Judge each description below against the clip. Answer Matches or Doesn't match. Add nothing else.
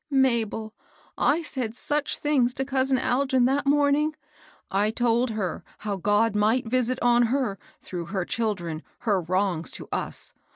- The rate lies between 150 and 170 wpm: Matches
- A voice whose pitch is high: Matches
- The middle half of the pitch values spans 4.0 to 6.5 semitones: Matches